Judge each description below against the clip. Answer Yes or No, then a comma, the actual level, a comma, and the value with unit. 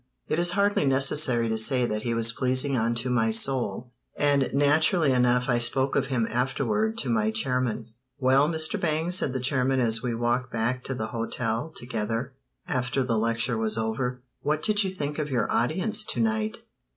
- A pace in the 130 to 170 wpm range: No, average, 185 wpm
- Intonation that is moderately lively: Yes, average, 4.0 semitones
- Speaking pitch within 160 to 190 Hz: No, low, 125 Hz